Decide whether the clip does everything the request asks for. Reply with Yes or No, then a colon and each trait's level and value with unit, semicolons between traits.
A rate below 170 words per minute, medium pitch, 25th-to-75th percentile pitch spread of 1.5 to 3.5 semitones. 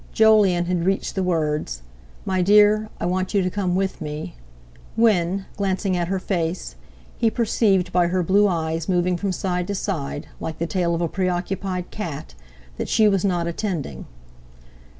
Yes: average, 160 wpm; medium, 180 Hz; narrow, 2.6 semitones